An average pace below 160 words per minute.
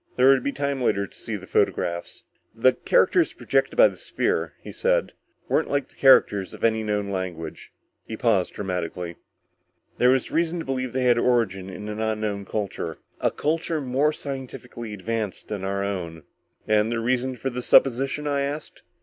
No: average, 175 wpm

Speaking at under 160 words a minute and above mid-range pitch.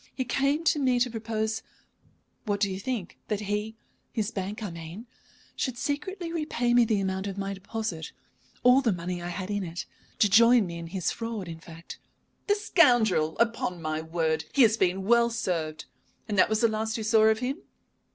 No: average, 200 wpm; high, 215 Hz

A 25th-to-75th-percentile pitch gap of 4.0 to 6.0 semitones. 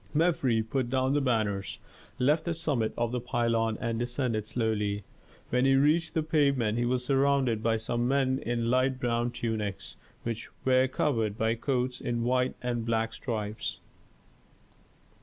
No: average, 2.7 semitones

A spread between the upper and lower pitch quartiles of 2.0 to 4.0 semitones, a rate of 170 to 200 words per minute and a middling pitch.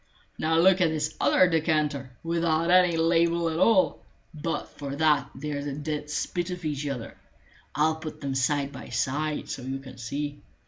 Yes: average, 2.8 semitones; average, 175 wpm; medium, 155 Hz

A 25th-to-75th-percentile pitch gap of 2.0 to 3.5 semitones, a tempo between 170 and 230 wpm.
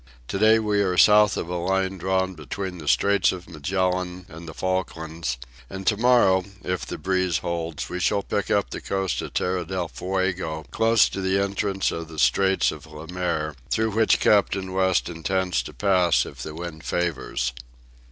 Yes: narrow, 2.5 semitones; average, 180 wpm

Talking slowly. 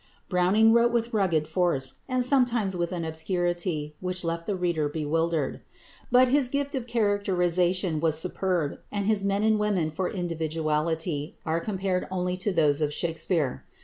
No: average, 155 wpm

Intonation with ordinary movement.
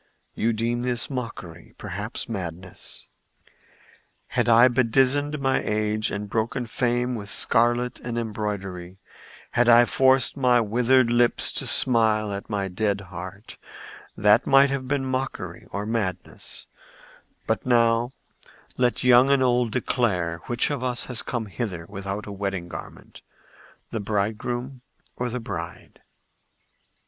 Yes: average, 3.3 semitones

